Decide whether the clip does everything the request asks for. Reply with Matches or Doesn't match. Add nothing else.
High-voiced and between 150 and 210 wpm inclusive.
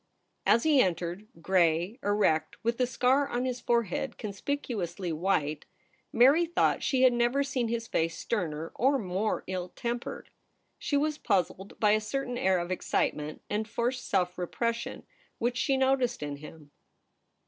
Matches